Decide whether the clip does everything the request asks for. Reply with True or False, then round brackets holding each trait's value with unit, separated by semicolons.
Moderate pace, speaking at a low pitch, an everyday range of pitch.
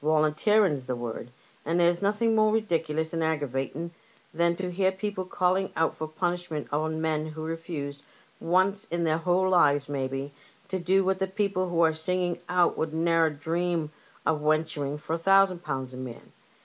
False (175 wpm; 165 Hz; 3.2 semitones)